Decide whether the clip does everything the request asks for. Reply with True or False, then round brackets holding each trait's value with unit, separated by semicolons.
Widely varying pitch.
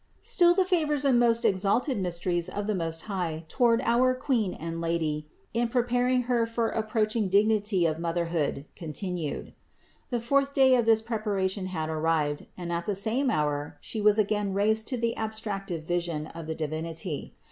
True (5.8 semitones)